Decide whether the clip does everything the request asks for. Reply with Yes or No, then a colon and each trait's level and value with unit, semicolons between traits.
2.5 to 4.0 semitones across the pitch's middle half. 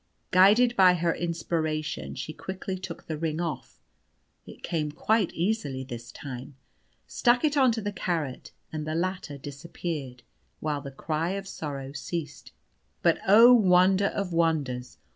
No: average, 4.5 semitones